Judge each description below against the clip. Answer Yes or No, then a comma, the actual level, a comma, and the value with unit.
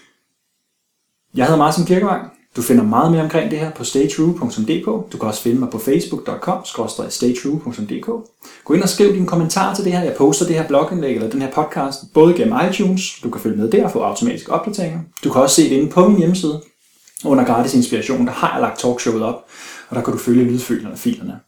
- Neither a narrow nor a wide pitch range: No, wide, 6.0 semitones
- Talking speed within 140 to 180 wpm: No, average, 210 wpm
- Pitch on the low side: No, medium, 165 Hz